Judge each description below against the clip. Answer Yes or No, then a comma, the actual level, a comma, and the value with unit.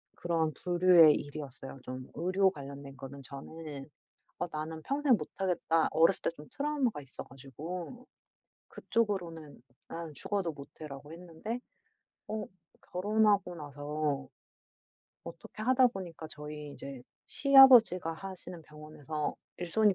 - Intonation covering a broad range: No, average, 4.7 semitones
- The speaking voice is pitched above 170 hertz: No, medium, 165 Hz